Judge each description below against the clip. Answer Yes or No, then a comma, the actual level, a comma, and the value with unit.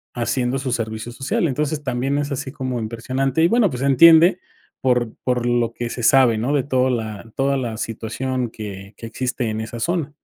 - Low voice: Yes, low, 125 Hz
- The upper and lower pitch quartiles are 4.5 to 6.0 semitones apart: No, average, 3.0 semitones